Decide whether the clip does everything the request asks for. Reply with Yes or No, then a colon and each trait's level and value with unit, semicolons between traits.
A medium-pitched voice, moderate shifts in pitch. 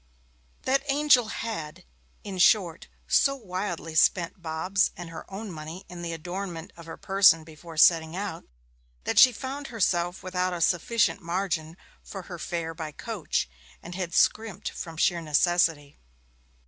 Yes: medium, 175 Hz; average, 3.3 semitones